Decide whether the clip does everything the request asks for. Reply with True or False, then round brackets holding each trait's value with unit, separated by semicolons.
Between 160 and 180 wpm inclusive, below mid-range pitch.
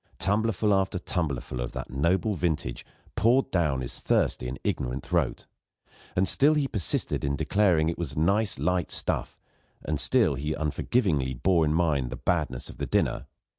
True (175 wpm; 85 Hz)